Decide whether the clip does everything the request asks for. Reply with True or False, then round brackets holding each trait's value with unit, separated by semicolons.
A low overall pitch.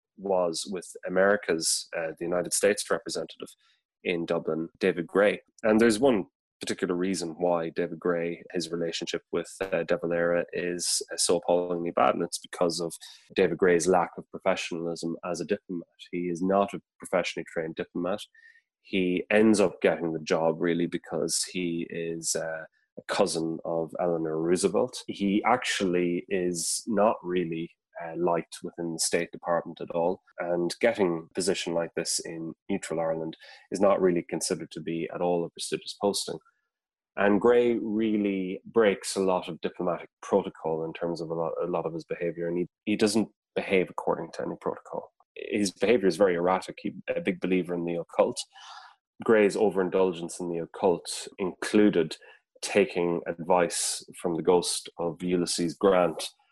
True (85 Hz)